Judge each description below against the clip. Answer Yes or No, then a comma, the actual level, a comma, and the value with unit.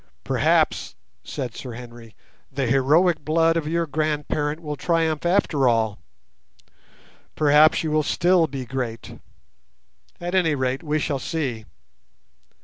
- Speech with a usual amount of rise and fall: Yes, average, 3.9 semitones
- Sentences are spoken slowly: Yes, slow, 125 wpm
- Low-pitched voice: No, medium, 150 Hz